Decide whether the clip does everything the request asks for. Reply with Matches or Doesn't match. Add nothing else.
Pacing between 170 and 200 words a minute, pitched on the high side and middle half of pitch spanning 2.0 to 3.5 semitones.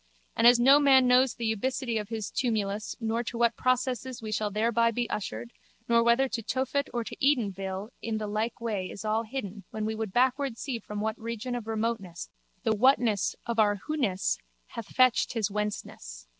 Matches